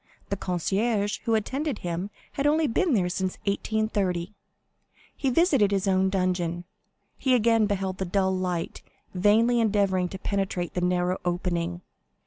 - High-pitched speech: Yes, high, 195 Hz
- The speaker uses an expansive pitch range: No, average, 3.4 semitones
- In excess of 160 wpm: No, average, 140 wpm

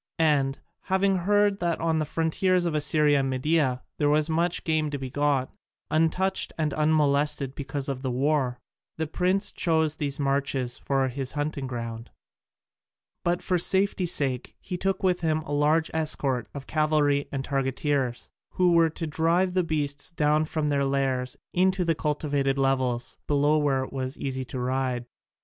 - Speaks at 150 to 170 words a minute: Yes, average, 165 wpm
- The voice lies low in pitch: No, medium, 150 Hz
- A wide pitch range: No, average, 3.3 semitones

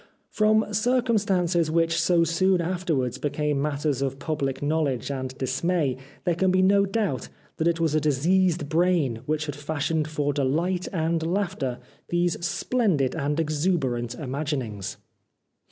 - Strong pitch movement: No, average, 4.2 semitones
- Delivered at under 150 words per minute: Yes, slow, 135 wpm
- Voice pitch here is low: No, medium, 160 Hz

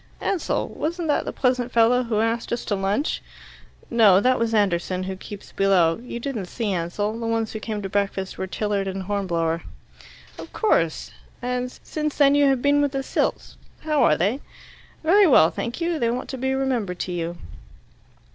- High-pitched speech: Yes, high, 225 Hz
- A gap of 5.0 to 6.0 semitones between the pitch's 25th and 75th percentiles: Yes, wide, 5.5 semitones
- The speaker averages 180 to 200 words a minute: Yes, average, 185 wpm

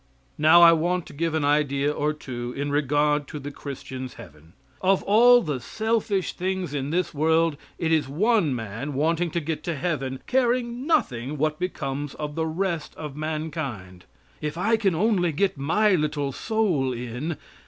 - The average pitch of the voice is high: No, medium, 155 Hz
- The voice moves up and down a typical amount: Yes, average, 4.3 semitones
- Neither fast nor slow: Yes, average, 170 wpm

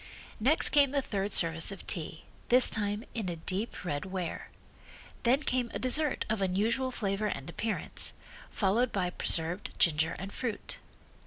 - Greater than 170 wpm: No, average, 155 wpm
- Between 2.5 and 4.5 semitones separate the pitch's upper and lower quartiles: No, average, 5.2 semitones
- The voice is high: Yes, high, 205 Hz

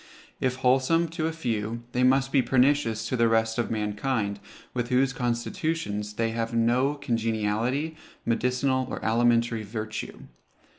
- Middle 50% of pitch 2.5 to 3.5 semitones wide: Yes, average, 2.9 semitones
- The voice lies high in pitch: No, low, 120 Hz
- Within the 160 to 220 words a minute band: No, average, 140 wpm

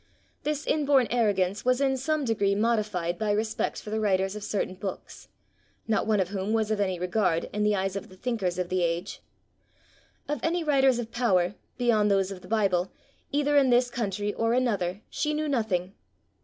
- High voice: Yes, high, 210 Hz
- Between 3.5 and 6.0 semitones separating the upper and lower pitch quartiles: Yes, average, 4.4 semitones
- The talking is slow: No, average, 190 wpm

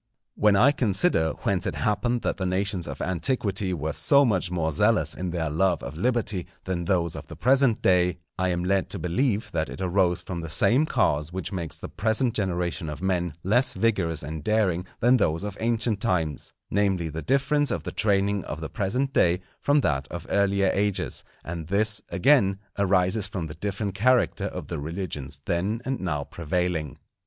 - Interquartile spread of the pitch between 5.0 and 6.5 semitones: No, average, 4.1 semitones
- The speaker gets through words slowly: No, average, 185 wpm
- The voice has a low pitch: Yes, very low, 95 Hz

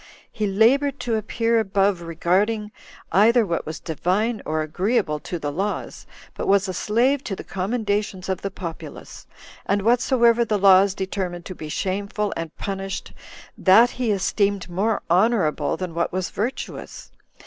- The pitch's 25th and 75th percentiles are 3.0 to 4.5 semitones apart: Yes, average, 3.3 semitones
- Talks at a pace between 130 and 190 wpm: Yes, average, 150 wpm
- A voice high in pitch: Yes, high, 200 Hz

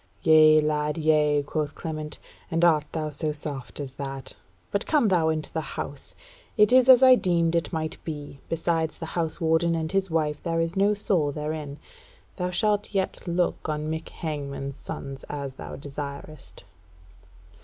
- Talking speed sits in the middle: Yes, average, 165 wpm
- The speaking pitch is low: No, medium, 155 Hz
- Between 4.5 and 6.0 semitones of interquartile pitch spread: No, narrow, 2.4 semitones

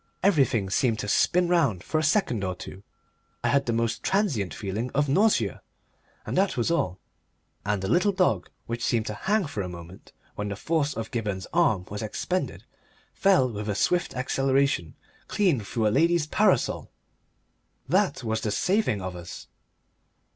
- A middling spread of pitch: No, wide, 8.7 semitones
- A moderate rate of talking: Yes, average, 170 wpm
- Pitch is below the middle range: Yes, low, 125 Hz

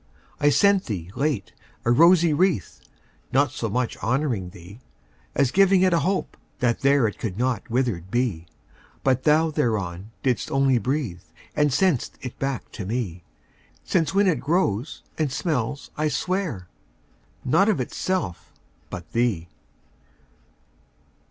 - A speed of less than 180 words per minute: Yes, slow, 135 wpm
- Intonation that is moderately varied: No, wide, 6.1 semitones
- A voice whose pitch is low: Yes, low, 130 Hz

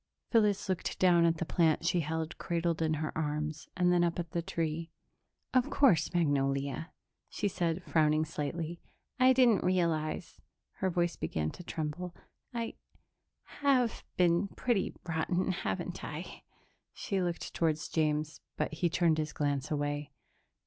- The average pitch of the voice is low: No, medium, 165 Hz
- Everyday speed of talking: Yes, average, 145 wpm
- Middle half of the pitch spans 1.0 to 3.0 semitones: Yes, average, 2.7 semitones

